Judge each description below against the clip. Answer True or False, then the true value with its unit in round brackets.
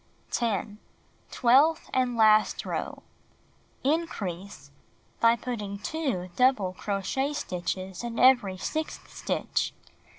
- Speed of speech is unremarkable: False (95 wpm)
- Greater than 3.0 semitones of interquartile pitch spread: True (5.1 semitones)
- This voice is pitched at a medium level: False (230 Hz)